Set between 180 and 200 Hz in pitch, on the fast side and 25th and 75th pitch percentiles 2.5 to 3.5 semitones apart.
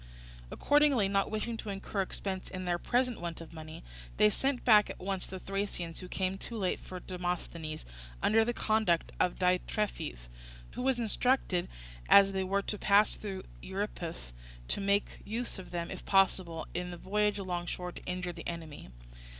No: high, 190 Hz; average, 175 wpm; average, 3.0 semitones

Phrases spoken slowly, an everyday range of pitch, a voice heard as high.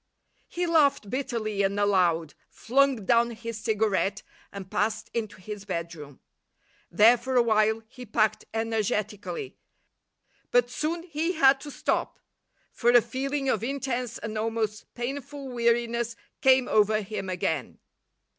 Yes: slow, 130 wpm; average, 3.7 semitones; high, 230 Hz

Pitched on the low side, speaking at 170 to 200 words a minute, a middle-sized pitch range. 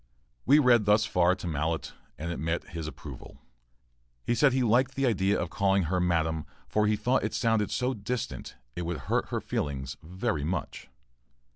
No: very low, 95 Hz; average, 180 wpm; wide, 6.0 semitones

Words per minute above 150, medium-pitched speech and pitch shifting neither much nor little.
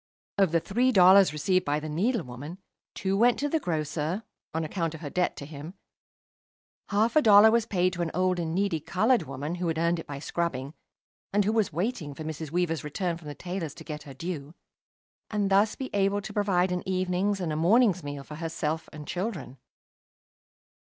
Yes: average, 200 wpm; medium, 175 Hz; average, 4.4 semitones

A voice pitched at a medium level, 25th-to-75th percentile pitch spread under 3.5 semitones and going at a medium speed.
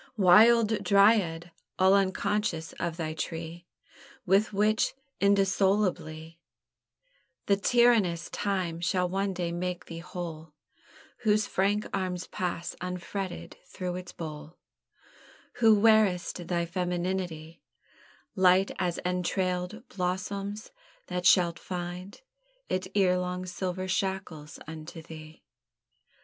No: medium, 180 Hz; narrow, 2.4 semitones; slow, 100 wpm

